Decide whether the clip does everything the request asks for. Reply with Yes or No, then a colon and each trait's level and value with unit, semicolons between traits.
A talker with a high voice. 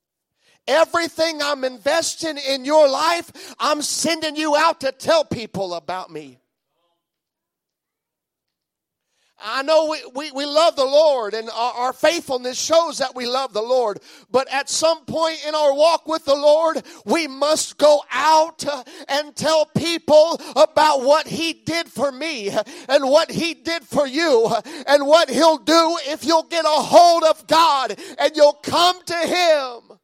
Yes: very high, 300 Hz